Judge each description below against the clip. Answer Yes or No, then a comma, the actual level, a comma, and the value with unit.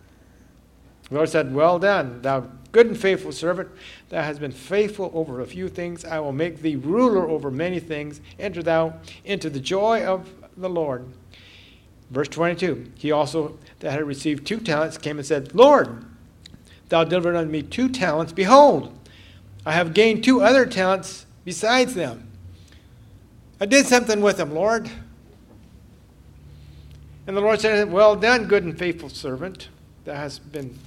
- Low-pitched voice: No, medium, 160 Hz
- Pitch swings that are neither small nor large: No, wide, 6.6 semitones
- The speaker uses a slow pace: No, average, 155 wpm